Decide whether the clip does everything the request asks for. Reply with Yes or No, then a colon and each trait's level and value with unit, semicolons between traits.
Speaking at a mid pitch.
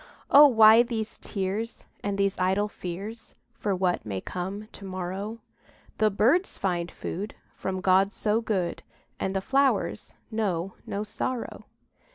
No: high, 200 Hz